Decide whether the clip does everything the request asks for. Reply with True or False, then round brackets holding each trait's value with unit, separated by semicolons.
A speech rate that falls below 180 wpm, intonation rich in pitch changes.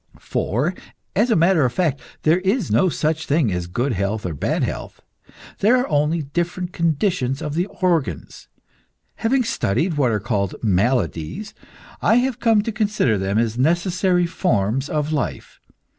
True (160 wpm; 7.9 semitones)